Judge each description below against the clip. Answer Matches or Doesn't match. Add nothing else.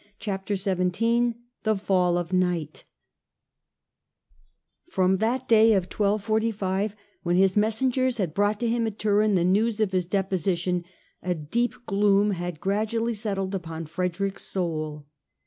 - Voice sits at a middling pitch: Doesn't match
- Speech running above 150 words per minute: Doesn't match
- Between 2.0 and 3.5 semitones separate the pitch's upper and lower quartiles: Matches